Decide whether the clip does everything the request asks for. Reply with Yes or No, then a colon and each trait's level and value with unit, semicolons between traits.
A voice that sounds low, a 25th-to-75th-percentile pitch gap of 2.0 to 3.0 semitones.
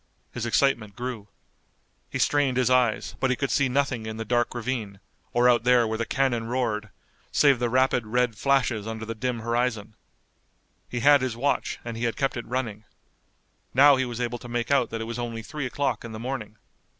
Yes: low, 120 Hz; narrow, 2.4 semitones